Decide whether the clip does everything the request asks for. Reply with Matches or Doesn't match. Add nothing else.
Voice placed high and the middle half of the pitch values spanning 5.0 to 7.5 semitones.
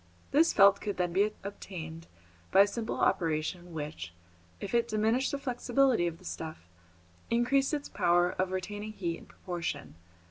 Matches